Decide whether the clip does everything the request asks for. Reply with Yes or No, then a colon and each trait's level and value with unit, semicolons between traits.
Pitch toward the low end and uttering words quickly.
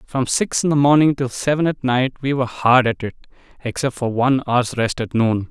Yes: low, 130 Hz; fast, 230 wpm